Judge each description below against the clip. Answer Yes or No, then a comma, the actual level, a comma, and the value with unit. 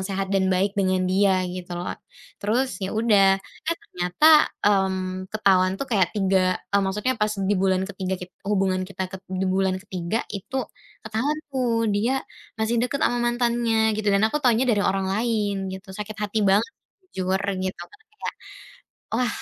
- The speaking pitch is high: Yes, high, 200 Hz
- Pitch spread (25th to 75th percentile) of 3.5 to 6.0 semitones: No, average, 3.0 semitones